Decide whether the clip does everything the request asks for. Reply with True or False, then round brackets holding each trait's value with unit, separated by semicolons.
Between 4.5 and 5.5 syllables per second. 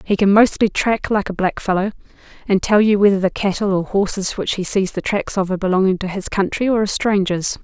False (5.9 syllables/s)